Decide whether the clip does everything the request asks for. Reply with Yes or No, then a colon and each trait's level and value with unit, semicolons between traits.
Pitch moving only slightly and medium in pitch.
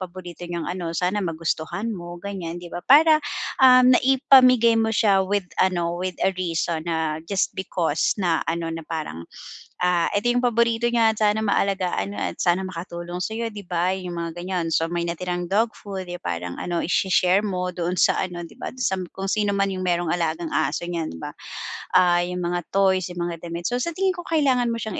No: average, 3.4 semitones; medium, 180 Hz